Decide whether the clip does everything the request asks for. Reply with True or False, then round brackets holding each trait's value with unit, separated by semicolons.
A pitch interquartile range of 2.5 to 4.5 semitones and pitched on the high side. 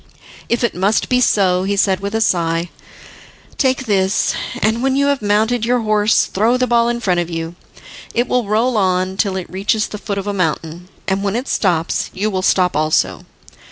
True (4.0 semitones; 200 Hz)